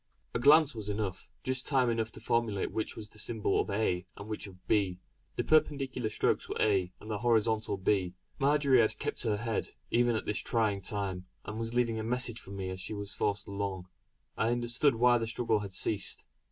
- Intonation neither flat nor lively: Yes, average, 3.0 semitones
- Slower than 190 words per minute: No, fast, 205 wpm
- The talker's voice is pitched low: Yes, low, 110 Hz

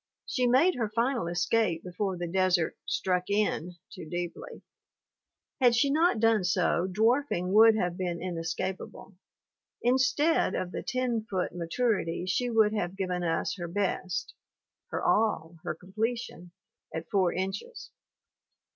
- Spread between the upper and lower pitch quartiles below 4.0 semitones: No, average, 4.4 semitones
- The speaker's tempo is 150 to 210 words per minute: No, slow, 135 wpm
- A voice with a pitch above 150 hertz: Yes, high, 190 Hz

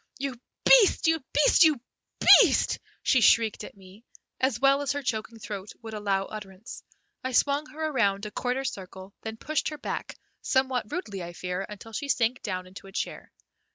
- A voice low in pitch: No, high, 225 Hz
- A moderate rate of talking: Yes, average, 180 wpm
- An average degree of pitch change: No, wide, 5.7 semitones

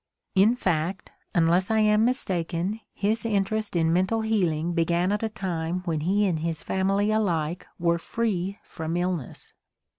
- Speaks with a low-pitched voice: No, medium, 185 Hz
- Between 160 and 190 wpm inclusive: No, average, 150 wpm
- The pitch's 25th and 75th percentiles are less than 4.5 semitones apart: Yes, average, 4.0 semitones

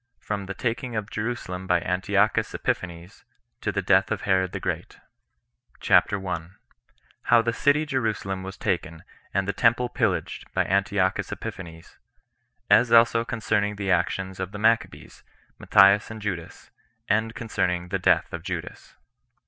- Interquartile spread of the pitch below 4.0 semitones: Yes, average, 3.2 semitones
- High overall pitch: No, low, 100 Hz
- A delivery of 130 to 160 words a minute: Yes, average, 145 wpm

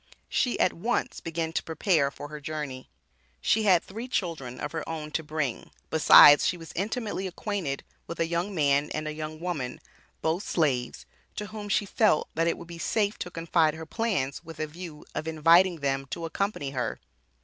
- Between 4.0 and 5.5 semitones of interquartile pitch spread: No, average, 3.5 semitones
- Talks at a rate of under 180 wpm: No, average, 190 wpm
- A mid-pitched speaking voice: Yes, medium, 165 Hz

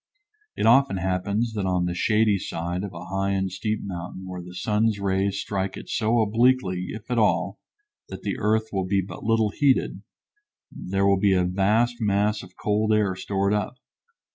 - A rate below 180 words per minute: No, average, 185 wpm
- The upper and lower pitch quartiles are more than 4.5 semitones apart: No, narrow, 2.6 semitones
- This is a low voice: Yes, low, 100 Hz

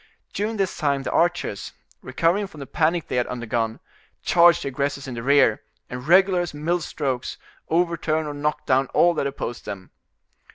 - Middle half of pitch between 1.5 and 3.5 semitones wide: No, average, 4.7 semitones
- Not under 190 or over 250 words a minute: No, average, 175 wpm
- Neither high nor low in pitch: Yes, medium, 150 Hz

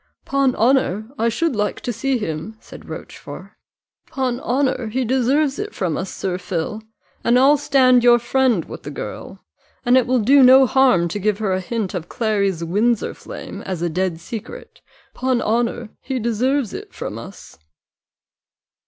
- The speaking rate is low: No, average, 170 wpm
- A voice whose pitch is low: No, high, 235 Hz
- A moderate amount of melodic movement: Yes, average, 4.7 semitones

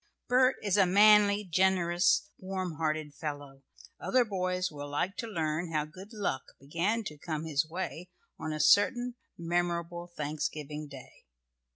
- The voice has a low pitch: No, medium, 175 Hz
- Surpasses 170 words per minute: No, average, 145 wpm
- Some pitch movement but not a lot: Yes, average, 4.1 semitones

